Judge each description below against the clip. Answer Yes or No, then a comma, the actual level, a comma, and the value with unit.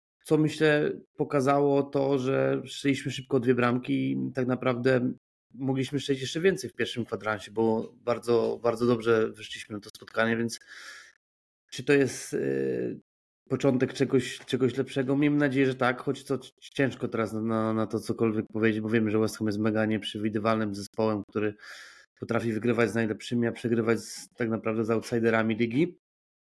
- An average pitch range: Yes, average, 3.4 semitones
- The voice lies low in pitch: Yes, low, 120 Hz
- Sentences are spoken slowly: No, fast, 160 wpm